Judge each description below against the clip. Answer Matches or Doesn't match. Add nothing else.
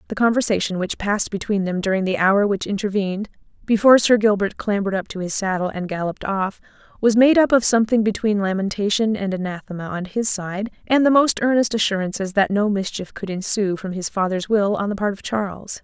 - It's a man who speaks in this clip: Doesn't match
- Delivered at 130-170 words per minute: Doesn't match